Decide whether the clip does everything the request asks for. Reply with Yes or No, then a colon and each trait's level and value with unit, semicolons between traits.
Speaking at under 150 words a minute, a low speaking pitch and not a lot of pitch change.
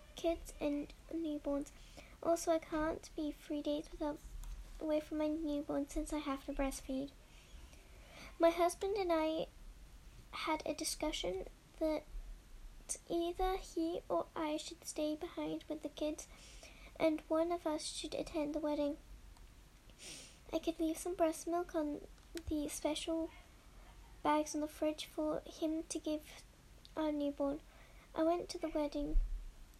No: average, 140 wpm; very high, 310 Hz; narrow, 1.6 semitones